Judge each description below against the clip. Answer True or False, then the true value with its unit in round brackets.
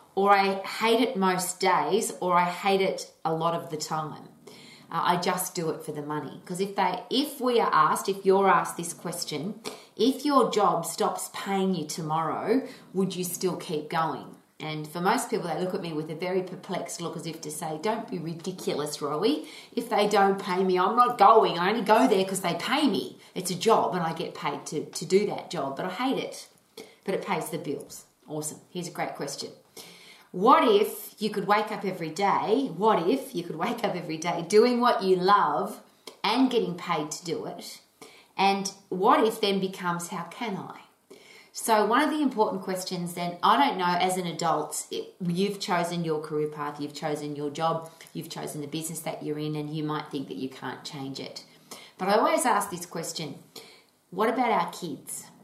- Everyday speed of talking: False (210 wpm)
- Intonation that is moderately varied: True (4.1 semitones)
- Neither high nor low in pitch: True (180 Hz)